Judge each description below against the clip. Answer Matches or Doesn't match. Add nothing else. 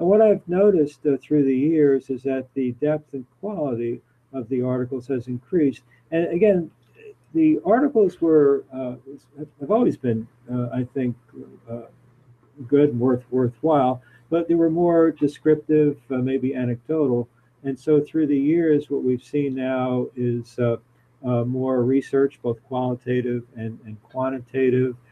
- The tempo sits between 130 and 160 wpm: Matches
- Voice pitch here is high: Doesn't match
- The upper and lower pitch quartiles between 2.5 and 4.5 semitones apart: Matches